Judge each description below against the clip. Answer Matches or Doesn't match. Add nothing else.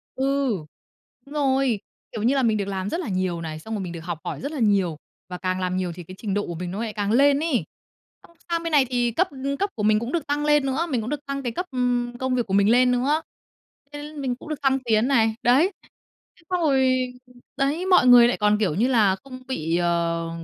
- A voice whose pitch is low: Doesn't match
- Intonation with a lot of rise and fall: Matches